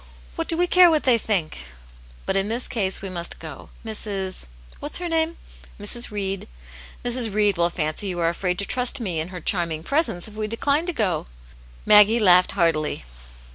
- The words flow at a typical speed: No, fast, 210 wpm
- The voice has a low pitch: No, high, 200 Hz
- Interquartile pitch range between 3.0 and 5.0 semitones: No, wide, 5.5 semitones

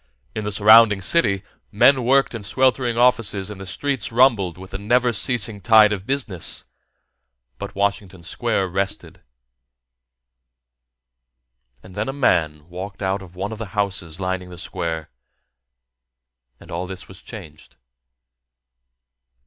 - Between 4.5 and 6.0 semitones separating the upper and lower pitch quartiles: No, average, 3.8 semitones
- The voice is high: No, low, 100 Hz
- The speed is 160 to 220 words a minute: No, slow, 135 wpm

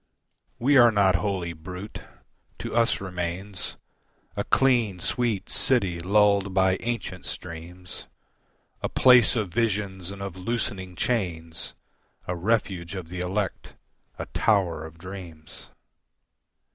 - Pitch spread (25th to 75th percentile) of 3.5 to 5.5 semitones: No, average, 3.1 semitones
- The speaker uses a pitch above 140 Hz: No, very low, 95 Hz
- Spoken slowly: Yes, slow, 120 wpm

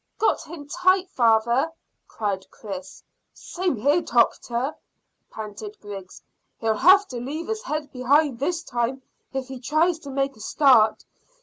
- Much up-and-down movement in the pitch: Yes, wide, 6.0 semitones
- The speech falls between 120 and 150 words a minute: Yes, average, 140 wpm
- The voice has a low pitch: No, very high, 265 Hz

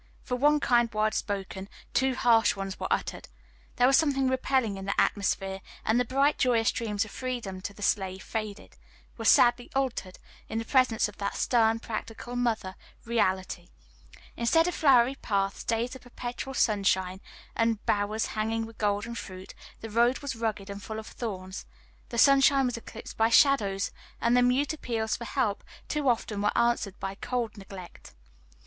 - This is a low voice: No, high, 225 Hz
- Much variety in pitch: No, average, 3.6 semitones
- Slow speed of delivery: No, average, 170 wpm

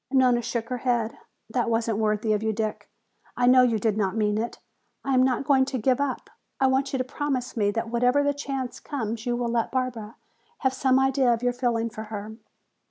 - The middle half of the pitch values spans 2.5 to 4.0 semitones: Yes, average, 2.9 semitones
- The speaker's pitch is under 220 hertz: No, high, 245 Hz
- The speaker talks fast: Yes, fast, 220 wpm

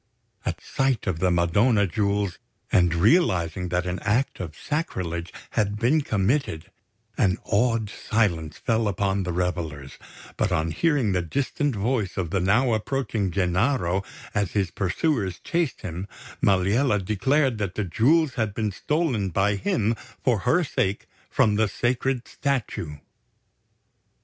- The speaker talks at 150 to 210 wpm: No, average, 140 wpm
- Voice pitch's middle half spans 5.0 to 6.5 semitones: Yes, average, 5.3 semitones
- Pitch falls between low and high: No, low, 100 Hz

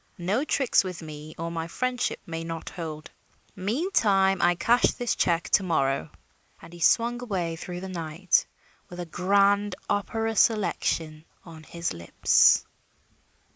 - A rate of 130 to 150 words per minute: Yes, average, 140 wpm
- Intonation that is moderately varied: Yes, average, 3.7 semitones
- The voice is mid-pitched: Yes, medium, 180 Hz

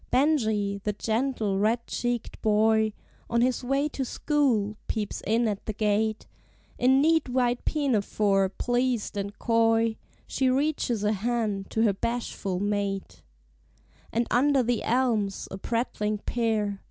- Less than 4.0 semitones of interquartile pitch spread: Yes, average, 3.1 semitones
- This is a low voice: No, high, 225 Hz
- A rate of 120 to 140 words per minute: Yes, slow, 135 wpm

